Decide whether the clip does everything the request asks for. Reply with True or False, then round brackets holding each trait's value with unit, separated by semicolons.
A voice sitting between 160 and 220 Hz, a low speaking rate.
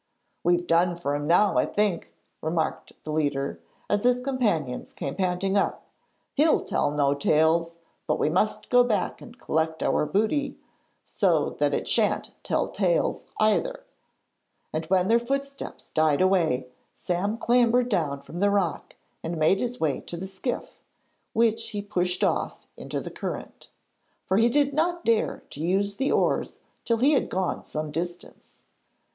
False (190 Hz; 160 wpm)